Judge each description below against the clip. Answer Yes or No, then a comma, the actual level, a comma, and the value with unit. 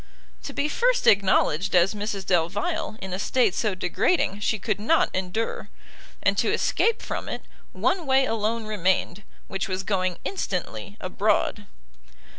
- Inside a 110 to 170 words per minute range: Yes, average, 145 wpm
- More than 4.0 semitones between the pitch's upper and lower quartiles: Yes, average, 5.0 semitones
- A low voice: No, high, 205 Hz